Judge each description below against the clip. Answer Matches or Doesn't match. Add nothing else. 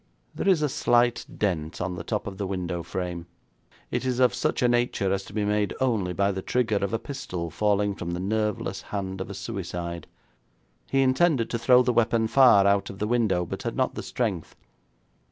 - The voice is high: Doesn't match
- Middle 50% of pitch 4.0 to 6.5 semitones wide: Matches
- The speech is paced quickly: Matches